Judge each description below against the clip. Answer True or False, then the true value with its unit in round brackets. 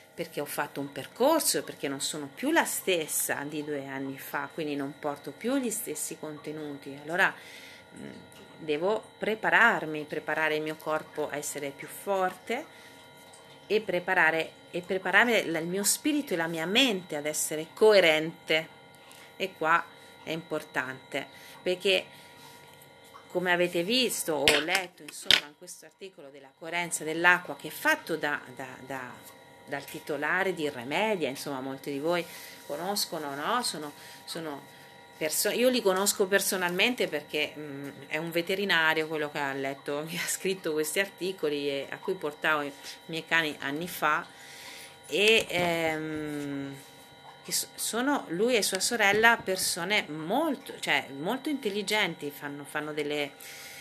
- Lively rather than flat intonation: False (4.4 semitones)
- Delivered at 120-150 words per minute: True (140 wpm)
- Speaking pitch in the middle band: True (160 Hz)